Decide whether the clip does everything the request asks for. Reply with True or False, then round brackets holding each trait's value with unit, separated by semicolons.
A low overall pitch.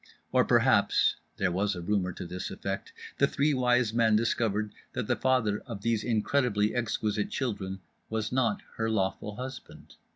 True (110 Hz)